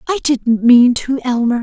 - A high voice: Yes, very high, 250 Hz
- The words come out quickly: No, average, 185 wpm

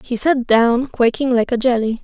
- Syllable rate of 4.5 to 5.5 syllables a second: Yes, 4.7 syllables/s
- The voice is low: No, high, 245 Hz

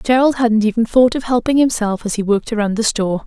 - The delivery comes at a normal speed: No, fast, 240 wpm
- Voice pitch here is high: Yes, high, 225 Hz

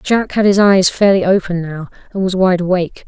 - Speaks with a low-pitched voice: No, medium, 185 Hz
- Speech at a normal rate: No, fast, 215 wpm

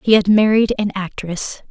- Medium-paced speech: Yes, average, 175 wpm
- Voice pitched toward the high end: Yes, high, 200 Hz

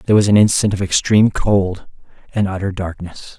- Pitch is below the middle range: Yes, low, 100 Hz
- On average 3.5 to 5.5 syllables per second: No, 5.8 syllables/s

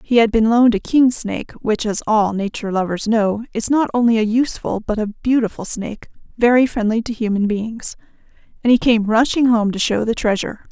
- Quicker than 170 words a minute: Yes, average, 200 wpm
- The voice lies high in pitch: Yes, high, 225 Hz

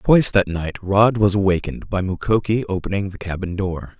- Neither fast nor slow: Yes, average, 180 wpm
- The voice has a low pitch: Yes, low, 100 Hz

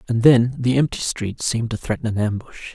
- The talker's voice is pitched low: Yes, low, 120 Hz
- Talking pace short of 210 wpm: No, fast, 220 wpm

